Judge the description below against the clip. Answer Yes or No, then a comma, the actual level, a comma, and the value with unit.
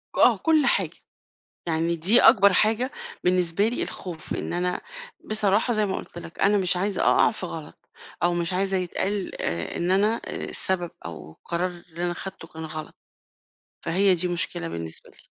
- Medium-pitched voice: Yes, medium, 180 Hz